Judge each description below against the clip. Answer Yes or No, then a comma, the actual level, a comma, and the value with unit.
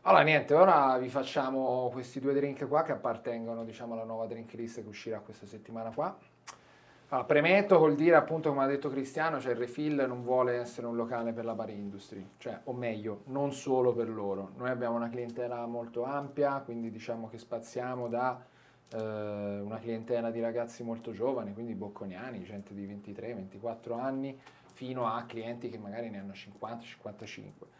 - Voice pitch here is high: No, low, 120 Hz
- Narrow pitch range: Yes, narrow, 2.3 semitones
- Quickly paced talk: Yes, fast, 175 wpm